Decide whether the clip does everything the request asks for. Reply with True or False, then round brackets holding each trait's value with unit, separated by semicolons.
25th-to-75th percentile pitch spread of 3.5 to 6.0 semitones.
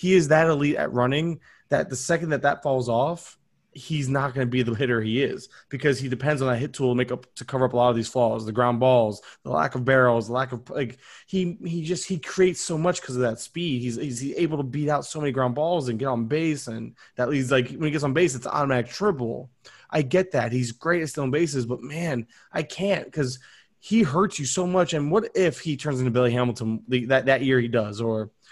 True (4.2 semitones)